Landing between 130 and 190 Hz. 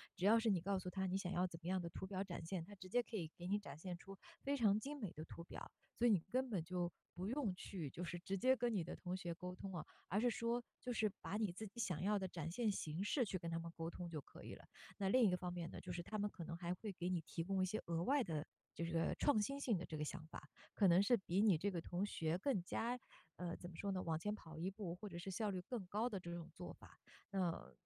Yes: medium, 185 Hz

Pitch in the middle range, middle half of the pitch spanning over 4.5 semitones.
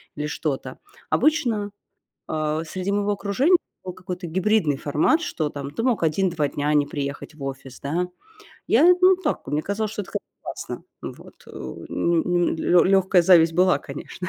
Yes: medium, 175 Hz; average, 5.2 semitones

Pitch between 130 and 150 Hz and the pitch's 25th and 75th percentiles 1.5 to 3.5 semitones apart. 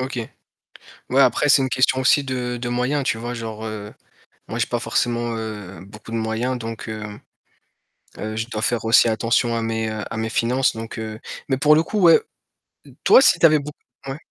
No: low, 120 Hz; average, 2.8 semitones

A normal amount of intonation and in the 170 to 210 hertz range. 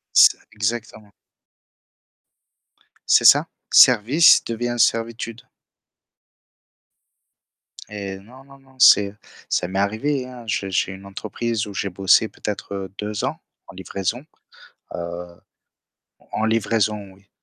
No: average, 3.1 semitones; low, 105 Hz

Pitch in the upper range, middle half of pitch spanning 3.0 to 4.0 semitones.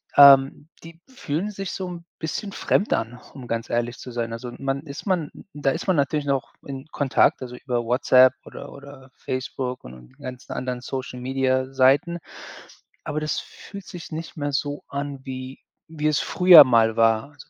No: low, 135 Hz; average, 3.3 semitones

